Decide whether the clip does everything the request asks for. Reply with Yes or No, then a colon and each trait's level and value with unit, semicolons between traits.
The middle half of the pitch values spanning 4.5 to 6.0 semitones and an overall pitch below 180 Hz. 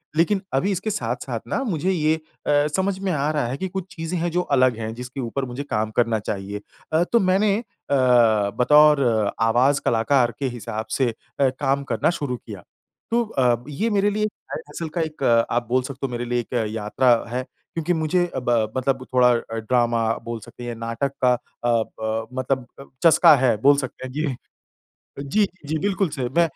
Yes: average, 5.3 semitones; low, 135 Hz